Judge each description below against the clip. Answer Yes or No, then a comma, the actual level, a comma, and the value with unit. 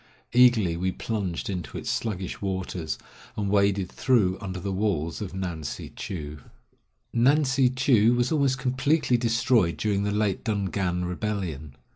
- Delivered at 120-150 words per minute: Yes, average, 145 wpm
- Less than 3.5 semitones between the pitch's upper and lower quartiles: No, average, 4.8 semitones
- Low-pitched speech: Yes, low, 100 Hz